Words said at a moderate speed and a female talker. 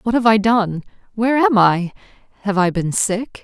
Yes: average, 190 wpm; female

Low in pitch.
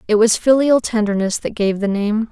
No: high, 220 Hz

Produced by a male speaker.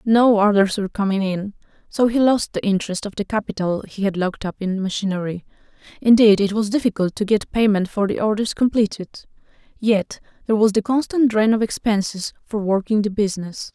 No: female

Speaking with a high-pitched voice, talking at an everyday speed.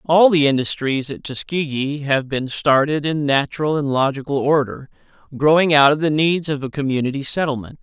No: medium, 145 Hz; average, 170 wpm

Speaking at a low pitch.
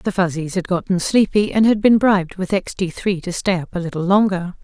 No: medium, 185 Hz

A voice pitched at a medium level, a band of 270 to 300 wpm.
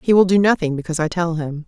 Yes: medium, 170 Hz; fast, 285 wpm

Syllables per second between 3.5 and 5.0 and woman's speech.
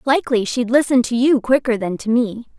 No: 5.4 syllables/s; female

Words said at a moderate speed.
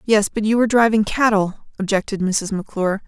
Yes: average, 175 wpm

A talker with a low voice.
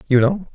No: medium, 150 Hz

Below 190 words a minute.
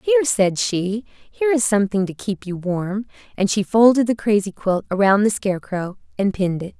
No: average, 195 wpm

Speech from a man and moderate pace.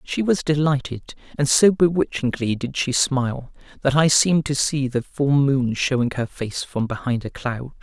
Yes: male; average, 190 wpm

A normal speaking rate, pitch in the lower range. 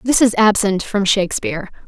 No: average, 160 wpm; high, 205 Hz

